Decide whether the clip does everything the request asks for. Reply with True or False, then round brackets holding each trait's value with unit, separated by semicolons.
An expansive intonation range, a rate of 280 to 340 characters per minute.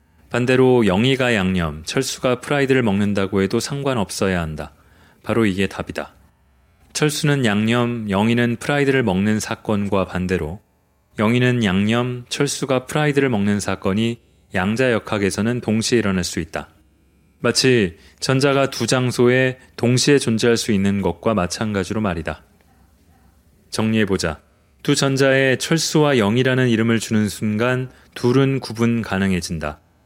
True (5.8 semitones; 300 characters per minute)